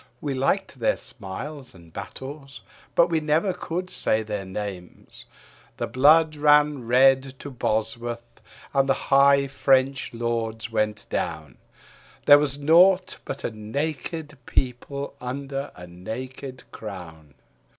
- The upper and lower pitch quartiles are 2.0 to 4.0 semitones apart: No, average, 4.7 semitones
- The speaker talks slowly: Yes, slow, 125 wpm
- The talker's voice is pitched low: Yes, low, 130 Hz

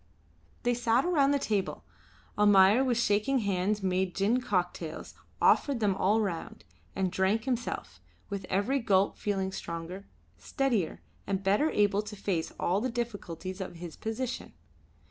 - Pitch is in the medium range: No, high, 205 Hz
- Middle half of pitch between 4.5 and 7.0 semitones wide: No, average, 3.9 semitones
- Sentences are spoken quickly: No, average, 145 wpm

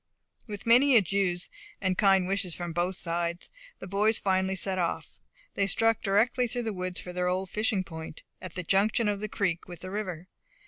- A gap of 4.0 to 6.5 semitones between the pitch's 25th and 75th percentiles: No, average, 2.7 semitones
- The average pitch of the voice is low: No, high, 190 Hz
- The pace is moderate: Yes, average, 190 wpm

